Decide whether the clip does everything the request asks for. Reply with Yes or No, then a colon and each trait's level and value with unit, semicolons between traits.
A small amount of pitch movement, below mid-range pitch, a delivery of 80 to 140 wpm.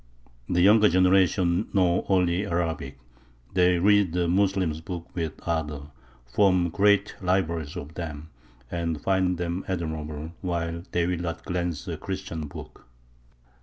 Yes: narrow, 2.3 semitones; very low, 85 Hz; slow, 135 wpm